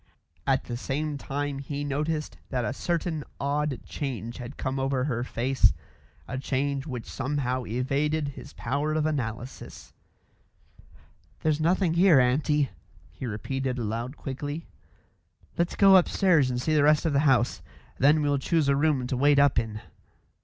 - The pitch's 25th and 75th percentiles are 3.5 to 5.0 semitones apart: No, average, 2.8 semitones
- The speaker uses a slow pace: No, average, 155 wpm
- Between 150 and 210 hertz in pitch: No, medium, 140 Hz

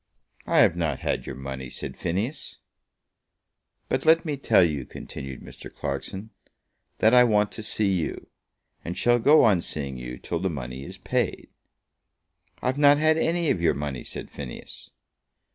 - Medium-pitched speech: No, very low, 95 Hz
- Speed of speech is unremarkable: Yes, average, 160 wpm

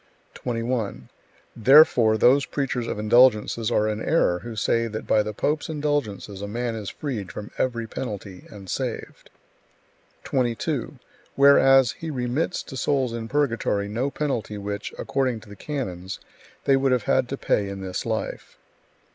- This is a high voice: No, low, 120 Hz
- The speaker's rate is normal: Yes, average, 155 wpm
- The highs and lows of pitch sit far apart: No, average, 4.2 semitones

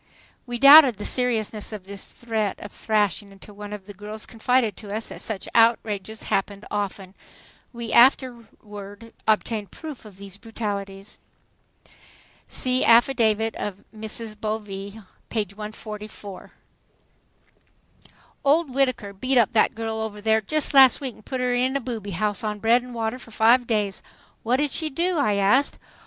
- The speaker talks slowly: No, average, 155 wpm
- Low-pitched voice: No, high, 220 Hz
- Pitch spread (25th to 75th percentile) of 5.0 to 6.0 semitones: No, average, 3.1 semitones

